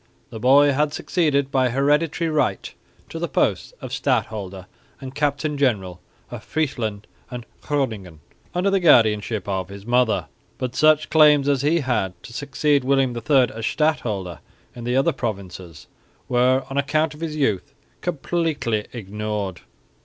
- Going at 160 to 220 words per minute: No, average, 145 wpm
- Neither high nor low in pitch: No, low, 130 Hz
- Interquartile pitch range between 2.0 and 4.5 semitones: No, wide, 5.5 semitones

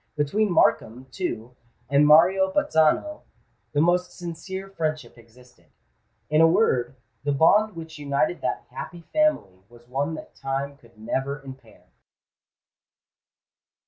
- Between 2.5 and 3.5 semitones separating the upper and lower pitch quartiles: No, average, 5.0 semitones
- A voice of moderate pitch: Yes, medium, 150 Hz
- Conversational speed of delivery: No, slow, 120 wpm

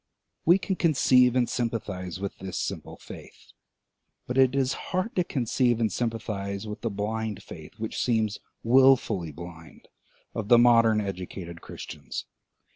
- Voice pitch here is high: No, low, 110 Hz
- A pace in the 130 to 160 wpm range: Yes, average, 140 wpm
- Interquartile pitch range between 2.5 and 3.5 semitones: No, average, 4.2 semitones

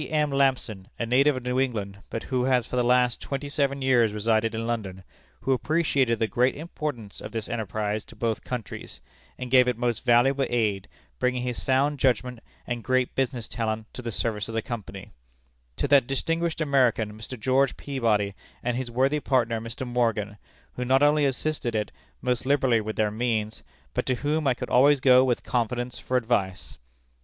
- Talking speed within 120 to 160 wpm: No, average, 185 wpm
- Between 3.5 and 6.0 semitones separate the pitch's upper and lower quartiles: No, average, 3.0 semitones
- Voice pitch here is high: No, low, 125 Hz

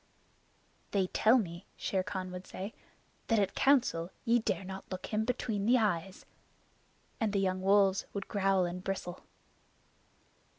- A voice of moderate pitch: No, high, 195 Hz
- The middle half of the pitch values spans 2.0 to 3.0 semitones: Yes, average, 2.7 semitones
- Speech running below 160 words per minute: Yes, average, 145 wpm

